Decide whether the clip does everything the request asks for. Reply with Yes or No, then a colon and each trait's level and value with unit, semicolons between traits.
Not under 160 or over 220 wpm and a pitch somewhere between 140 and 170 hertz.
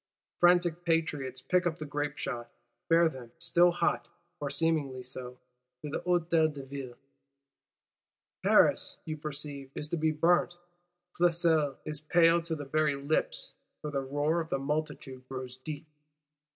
No: average, 145 wpm; medium, 150 Hz